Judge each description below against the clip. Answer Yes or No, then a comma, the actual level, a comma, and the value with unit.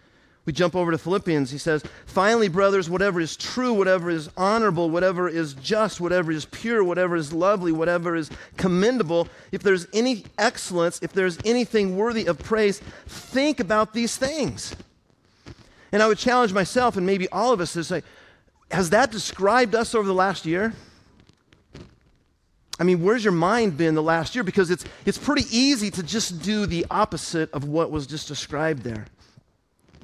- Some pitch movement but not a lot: Yes, average, 4.6 semitones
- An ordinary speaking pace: Yes, average, 170 wpm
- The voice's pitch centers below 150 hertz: No, medium, 185 Hz